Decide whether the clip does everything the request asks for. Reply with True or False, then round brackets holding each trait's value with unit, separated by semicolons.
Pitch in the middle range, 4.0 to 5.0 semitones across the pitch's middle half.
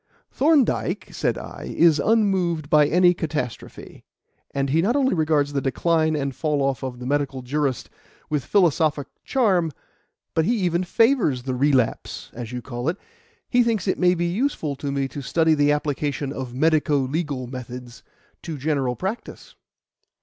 True (150 Hz; 4.3 semitones)